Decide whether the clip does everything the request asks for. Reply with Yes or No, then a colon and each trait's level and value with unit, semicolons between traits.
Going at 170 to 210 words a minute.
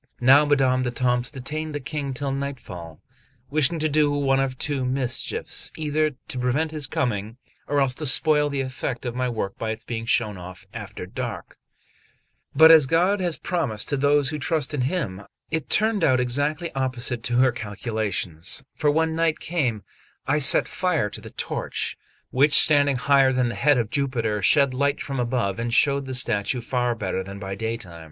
Yes: average, 185 wpm